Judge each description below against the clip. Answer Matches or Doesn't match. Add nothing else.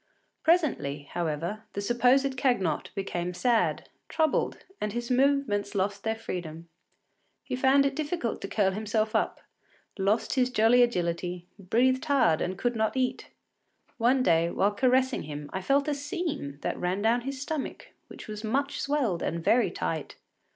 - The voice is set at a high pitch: Matches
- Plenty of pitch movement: Matches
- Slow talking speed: Doesn't match